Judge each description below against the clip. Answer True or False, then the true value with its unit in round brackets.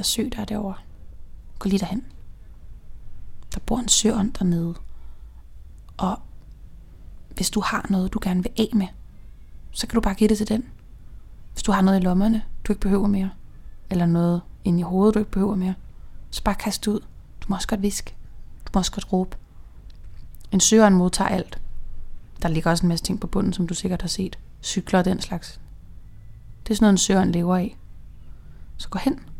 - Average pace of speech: True (200 wpm)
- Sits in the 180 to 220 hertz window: True (185 Hz)